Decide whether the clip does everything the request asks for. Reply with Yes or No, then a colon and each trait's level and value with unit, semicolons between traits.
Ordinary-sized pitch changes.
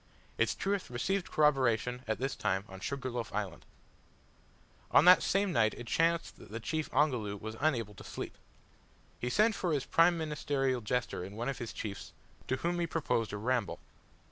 No: wide, 6.4 semitones